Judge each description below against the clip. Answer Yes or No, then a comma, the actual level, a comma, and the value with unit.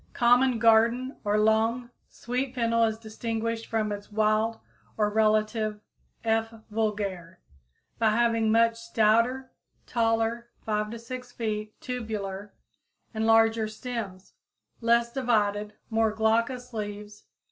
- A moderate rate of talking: No, slow, 120 wpm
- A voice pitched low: No, high, 225 Hz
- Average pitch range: No, narrow, 1.6 semitones